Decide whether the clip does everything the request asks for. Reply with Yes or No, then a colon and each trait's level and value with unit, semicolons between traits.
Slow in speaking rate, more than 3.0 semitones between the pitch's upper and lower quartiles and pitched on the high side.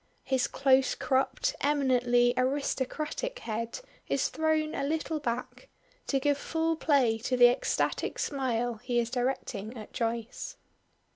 Yes: slow, 130 wpm; average, 3.5 semitones; very high, 260 Hz